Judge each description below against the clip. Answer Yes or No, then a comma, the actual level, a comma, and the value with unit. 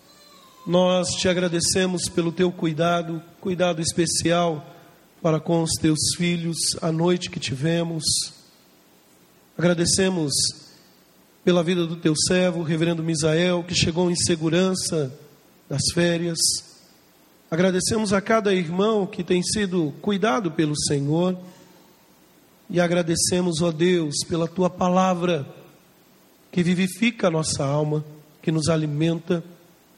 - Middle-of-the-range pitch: Yes, medium, 170 Hz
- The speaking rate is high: No, slow, 110 wpm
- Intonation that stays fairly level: Yes, narrow, 1.9 semitones